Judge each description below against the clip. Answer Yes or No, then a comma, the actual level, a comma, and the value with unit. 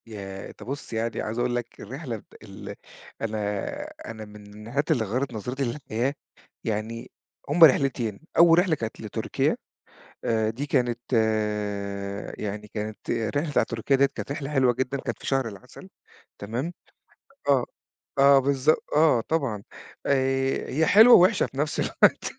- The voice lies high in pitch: No, low, 125 Hz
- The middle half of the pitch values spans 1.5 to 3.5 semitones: No, average, 4.2 semitones